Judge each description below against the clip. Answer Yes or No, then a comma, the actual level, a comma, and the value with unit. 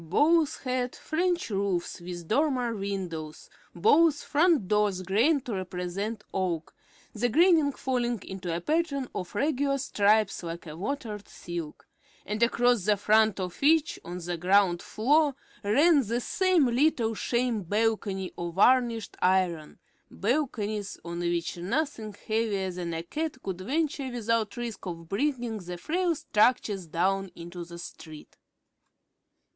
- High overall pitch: Yes, high, 215 Hz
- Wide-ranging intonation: Yes, wide, 6.5 semitones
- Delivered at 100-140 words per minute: Yes, slow, 135 wpm